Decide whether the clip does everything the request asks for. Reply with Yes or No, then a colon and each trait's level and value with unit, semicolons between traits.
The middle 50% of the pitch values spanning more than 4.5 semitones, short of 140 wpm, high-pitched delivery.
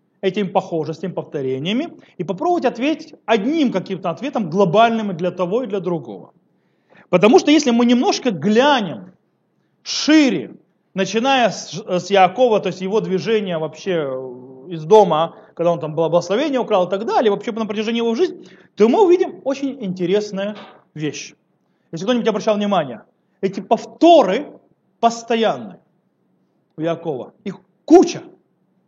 Yes: average, 5.0 semitones; average, 130 wpm; high, 205 Hz